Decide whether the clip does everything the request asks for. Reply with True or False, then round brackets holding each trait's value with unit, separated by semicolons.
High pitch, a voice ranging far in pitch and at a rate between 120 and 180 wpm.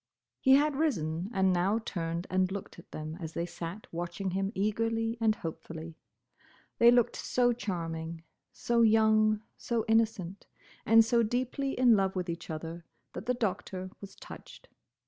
False (200 Hz; 4.8 semitones; 155 wpm)